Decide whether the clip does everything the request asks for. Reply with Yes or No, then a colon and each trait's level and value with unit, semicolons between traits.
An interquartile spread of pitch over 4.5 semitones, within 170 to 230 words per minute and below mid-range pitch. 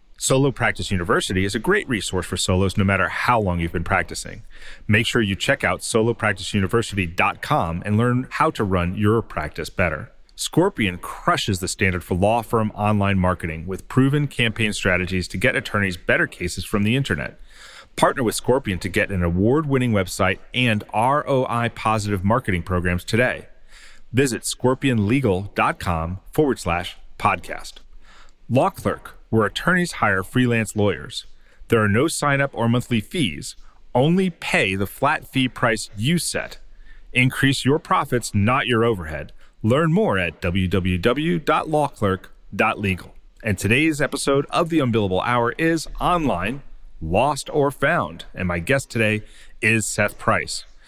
No: average, 5.2 semitones; average, 145 wpm; low, 110 Hz